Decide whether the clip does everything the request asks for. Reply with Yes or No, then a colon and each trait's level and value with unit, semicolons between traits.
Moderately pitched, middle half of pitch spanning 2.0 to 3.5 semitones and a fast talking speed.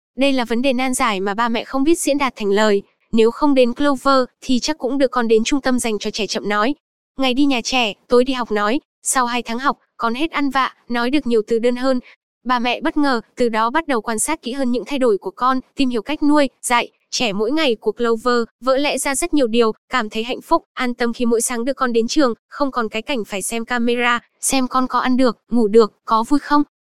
No: high, 245 Hz; average, 2.8 semitones; fast, 260 wpm